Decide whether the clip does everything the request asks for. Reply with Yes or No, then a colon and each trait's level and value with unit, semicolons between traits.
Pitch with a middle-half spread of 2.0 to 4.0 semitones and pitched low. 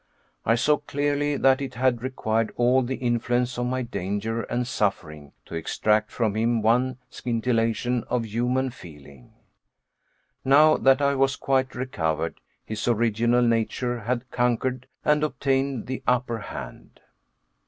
Yes: narrow, 2.6 semitones; low, 120 Hz